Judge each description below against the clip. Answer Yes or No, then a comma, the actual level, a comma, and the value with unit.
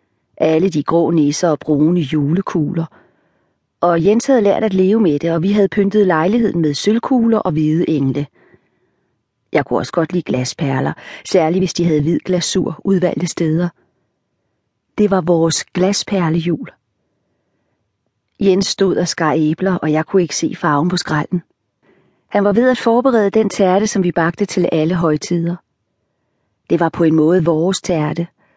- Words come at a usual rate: Yes, average, 160 wpm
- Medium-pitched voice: Yes, medium, 170 Hz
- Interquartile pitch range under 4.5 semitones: Yes, average, 4.0 semitones